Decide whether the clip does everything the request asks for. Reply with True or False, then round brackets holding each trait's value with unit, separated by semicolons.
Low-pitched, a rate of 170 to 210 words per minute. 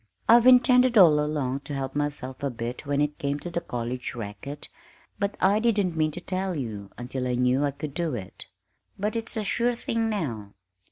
False (150 Hz; 200 wpm)